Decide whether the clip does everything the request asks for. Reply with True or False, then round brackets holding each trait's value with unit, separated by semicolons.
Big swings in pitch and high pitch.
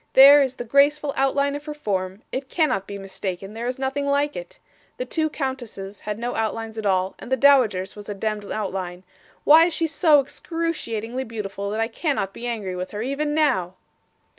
True (5.9 semitones; 240 Hz)